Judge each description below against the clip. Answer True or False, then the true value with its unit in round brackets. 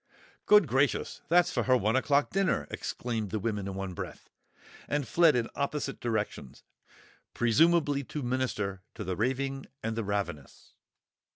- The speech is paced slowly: False (155 wpm)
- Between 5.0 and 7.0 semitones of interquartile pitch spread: True (5.3 semitones)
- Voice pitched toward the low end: True (125 Hz)